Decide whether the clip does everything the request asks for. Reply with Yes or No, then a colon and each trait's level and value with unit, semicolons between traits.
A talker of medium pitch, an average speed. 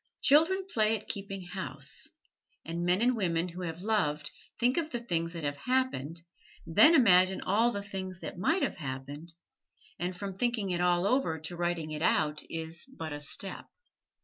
Yes: medium, 180 Hz; average, 175 wpm